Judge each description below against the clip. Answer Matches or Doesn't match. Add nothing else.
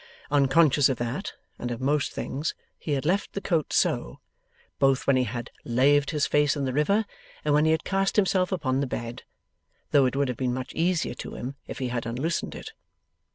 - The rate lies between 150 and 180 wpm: Doesn't match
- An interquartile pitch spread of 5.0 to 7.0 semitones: Doesn't match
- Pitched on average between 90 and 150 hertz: Matches